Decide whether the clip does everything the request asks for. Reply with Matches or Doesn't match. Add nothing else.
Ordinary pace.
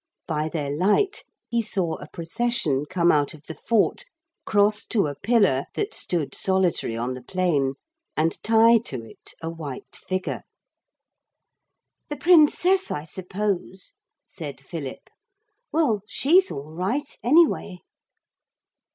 Doesn't match